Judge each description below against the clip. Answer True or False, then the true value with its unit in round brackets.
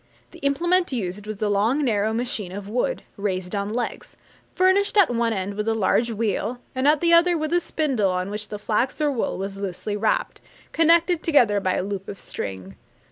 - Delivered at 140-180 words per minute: False (200 wpm)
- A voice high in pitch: True (220 Hz)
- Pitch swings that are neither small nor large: False (6.8 semitones)